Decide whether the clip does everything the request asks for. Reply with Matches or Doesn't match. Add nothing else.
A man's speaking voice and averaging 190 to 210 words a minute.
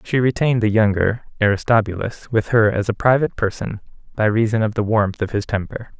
Matches